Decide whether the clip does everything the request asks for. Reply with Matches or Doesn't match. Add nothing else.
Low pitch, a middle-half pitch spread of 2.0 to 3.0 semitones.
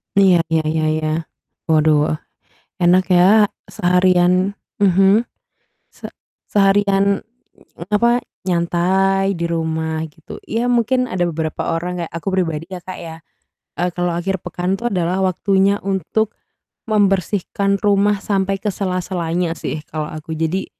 Doesn't match